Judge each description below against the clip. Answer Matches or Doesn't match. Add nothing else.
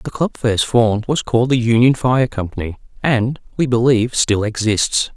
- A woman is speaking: Doesn't match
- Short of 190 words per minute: Matches